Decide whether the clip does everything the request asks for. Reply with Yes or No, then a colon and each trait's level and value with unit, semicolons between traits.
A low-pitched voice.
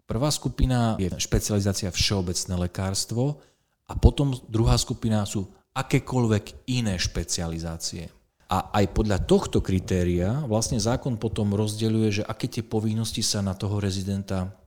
Yes: low, 105 Hz